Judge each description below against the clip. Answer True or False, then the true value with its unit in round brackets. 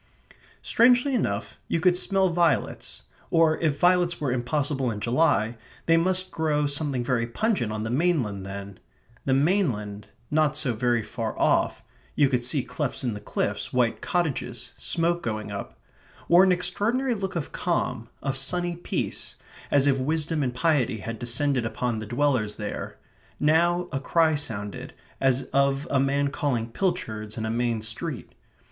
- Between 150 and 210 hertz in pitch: False (140 Hz)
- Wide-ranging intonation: True (6.1 semitones)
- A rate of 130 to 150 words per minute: False (160 wpm)